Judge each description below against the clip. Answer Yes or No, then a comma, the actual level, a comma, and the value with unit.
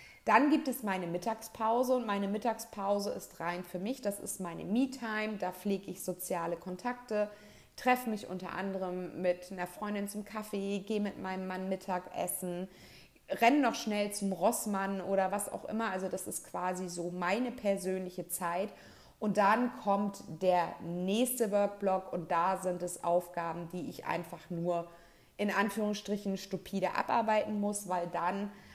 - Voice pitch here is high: Yes, high, 195 Hz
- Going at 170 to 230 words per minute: No, average, 155 wpm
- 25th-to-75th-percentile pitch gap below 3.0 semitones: Yes, narrow, 2.6 semitones